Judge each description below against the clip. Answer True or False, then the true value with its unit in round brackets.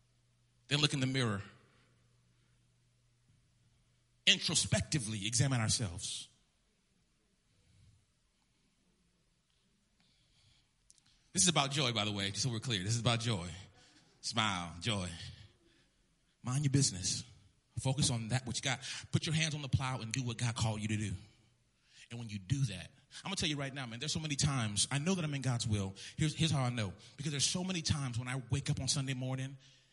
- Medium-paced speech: True (175 wpm)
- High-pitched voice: False (120 Hz)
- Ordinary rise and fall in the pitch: True (4.0 semitones)